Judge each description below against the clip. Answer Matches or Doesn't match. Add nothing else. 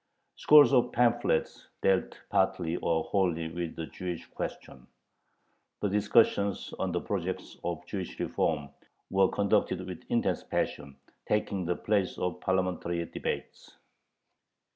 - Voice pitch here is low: Matches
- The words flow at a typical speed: Doesn't match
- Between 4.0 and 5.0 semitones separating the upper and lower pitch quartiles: Doesn't match